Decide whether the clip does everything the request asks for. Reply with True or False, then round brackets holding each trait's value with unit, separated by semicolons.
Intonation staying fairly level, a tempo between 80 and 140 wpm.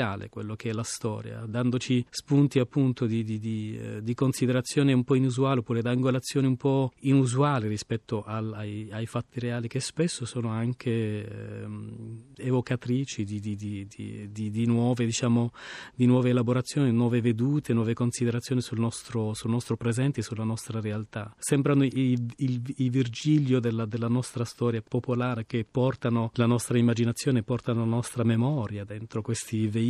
False (2.1 semitones; 155 wpm)